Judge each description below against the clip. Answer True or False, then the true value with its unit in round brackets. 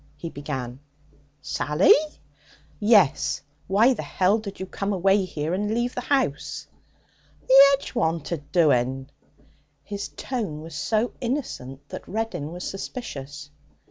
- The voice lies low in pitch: False (185 Hz)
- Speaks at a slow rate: True (125 wpm)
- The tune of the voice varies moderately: False (7.3 semitones)